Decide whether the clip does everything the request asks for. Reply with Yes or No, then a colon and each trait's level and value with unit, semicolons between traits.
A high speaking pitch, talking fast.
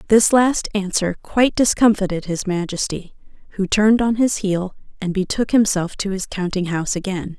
No: high, 195 Hz; average, 160 wpm